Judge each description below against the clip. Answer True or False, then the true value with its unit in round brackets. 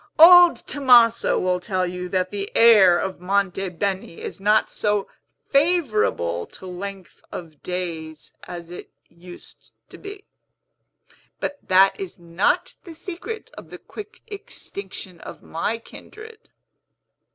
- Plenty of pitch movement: True (6.6 semitones)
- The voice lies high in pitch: True (195 Hz)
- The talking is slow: True (130 wpm)